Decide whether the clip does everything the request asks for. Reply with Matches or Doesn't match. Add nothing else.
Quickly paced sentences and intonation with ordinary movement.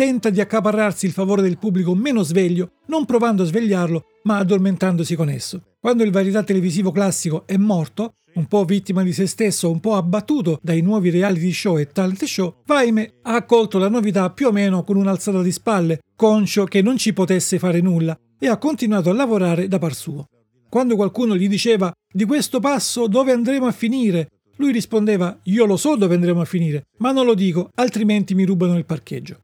Matches